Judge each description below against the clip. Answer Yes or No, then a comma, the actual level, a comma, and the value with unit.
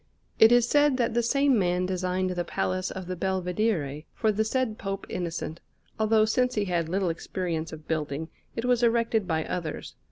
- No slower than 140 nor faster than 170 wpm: No, average, 185 wpm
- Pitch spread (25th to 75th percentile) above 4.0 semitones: Yes, average, 5.1 semitones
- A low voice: No, high, 190 Hz